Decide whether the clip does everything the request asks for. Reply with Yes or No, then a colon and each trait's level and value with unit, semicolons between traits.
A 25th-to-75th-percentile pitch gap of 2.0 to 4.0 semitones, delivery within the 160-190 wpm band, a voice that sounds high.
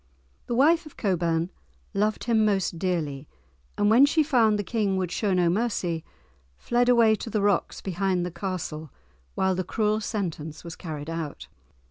No: average, 4.5 semitones; average, 165 wpm; high, 195 Hz